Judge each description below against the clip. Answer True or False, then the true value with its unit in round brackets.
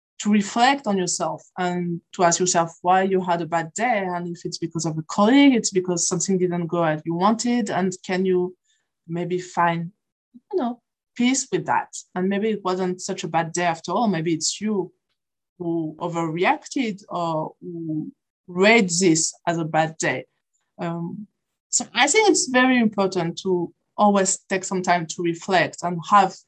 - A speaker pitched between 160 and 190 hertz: True (185 Hz)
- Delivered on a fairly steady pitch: False (3.5 semitones)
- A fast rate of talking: False (175 wpm)